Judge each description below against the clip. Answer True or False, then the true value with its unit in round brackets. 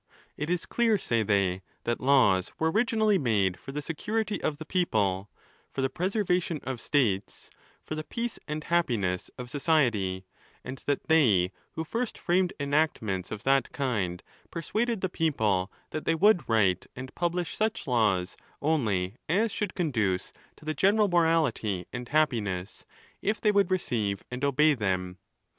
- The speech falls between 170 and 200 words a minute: False (160 wpm)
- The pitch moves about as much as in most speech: False (9.0 semitones)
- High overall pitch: False (140 Hz)